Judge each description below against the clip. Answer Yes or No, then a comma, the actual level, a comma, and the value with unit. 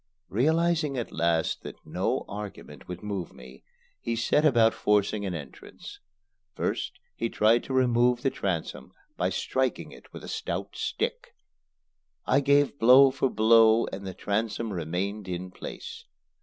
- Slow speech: No, average, 145 wpm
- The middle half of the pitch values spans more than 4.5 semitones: Yes, average, 5.3 semitones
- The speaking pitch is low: Yes, low, 115 Hz